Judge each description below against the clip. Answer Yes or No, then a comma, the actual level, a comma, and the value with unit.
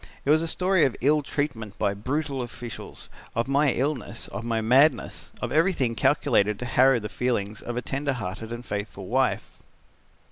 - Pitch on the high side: No, low, 125 Hz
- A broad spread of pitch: No, average, 4.2 semitones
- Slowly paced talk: No, average, 175 wpm